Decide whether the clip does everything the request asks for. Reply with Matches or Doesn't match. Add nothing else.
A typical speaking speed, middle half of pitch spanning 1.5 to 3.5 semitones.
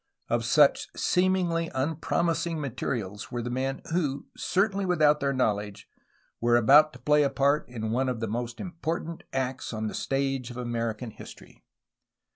Doesn't match